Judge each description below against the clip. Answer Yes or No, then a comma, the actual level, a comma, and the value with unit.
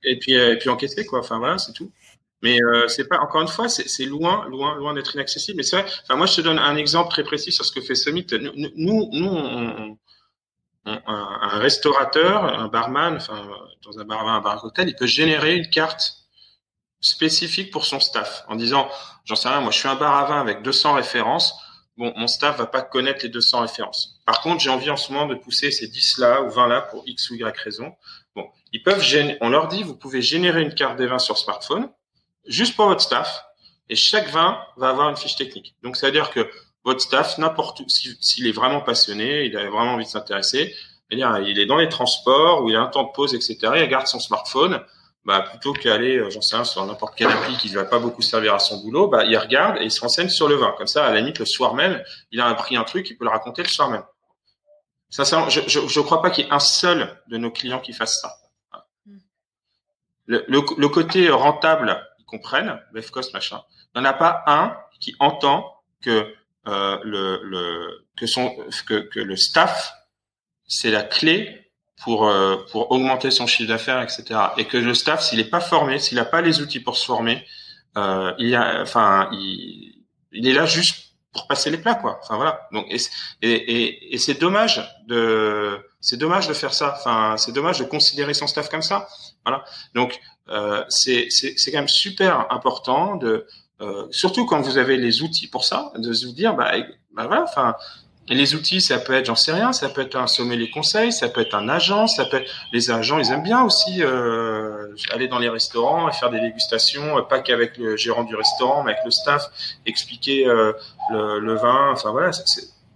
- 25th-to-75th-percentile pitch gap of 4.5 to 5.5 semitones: Yes, average, 5.2 semitones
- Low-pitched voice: Yes, low, 130 Hz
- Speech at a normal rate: No, fast, 225 wpm